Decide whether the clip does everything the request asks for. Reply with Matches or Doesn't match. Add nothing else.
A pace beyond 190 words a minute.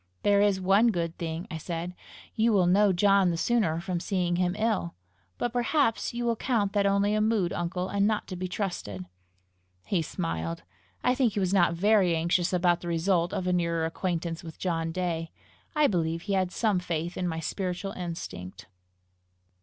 Doesn't match